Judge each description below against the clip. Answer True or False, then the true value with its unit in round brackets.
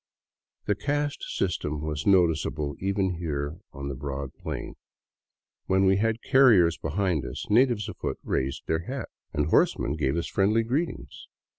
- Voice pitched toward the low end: True (90 Hz)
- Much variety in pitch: True (6.2 semitones)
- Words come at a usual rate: True (145 wpm)